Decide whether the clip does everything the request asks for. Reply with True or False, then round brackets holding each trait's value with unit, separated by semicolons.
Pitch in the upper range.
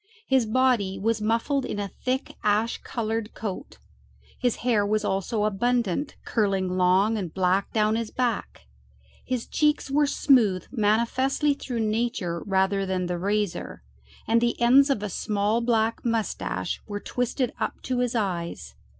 True (220 Hz)